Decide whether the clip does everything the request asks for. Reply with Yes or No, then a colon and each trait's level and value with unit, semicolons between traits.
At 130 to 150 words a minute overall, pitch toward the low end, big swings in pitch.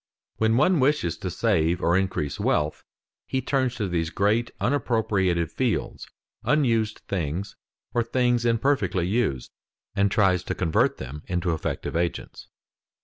Yes: slow, 135 wpm; low, 100 Hz; wide, 5.7 semitones